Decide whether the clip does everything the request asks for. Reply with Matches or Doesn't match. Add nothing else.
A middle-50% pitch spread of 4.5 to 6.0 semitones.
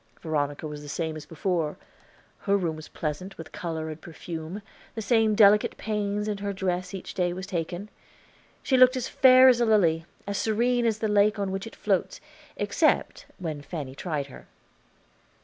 Matches